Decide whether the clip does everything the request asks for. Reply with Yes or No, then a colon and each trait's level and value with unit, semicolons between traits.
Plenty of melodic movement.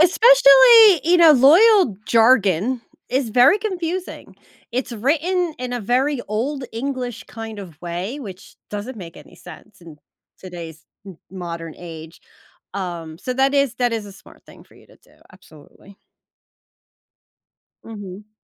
Yes: wide, 7.6 semitones